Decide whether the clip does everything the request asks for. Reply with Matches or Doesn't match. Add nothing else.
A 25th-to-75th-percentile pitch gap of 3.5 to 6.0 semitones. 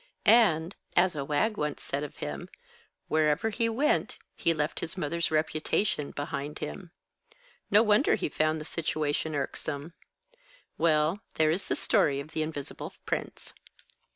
Doesn't match